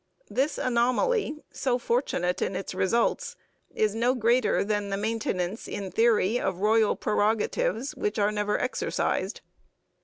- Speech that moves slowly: Yes, slow, 130 wpm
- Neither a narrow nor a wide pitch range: Yes, average, 3.0 semitones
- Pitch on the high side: Yes, high, 220 Hz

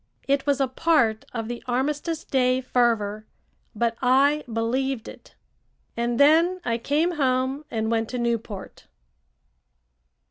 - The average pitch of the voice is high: Yes, very high, 255 Hz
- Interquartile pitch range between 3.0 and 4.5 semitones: Yes, average, 3.6 semitones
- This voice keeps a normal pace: No, slow, 130 wpm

